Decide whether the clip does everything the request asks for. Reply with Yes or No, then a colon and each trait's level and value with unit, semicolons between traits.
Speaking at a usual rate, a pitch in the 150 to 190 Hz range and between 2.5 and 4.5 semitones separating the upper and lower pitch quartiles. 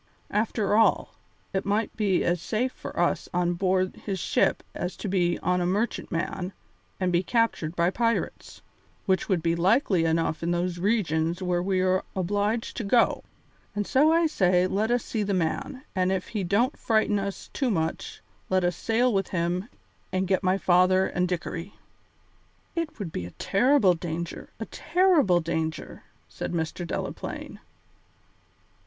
Yes: average, 160 wpm; medium, 185 Hz; average, 3.6 semitones